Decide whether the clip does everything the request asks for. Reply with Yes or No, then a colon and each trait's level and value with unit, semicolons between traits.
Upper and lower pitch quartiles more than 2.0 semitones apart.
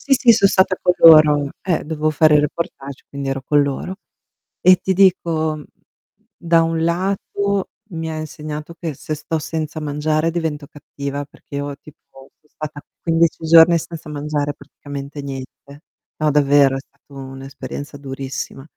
Yes: narrow, 2.5 semitones